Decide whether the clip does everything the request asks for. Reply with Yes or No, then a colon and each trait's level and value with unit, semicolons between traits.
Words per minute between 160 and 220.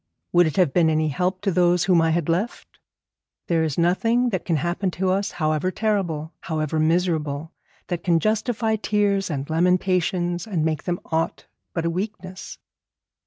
Yes: average, 165 wpm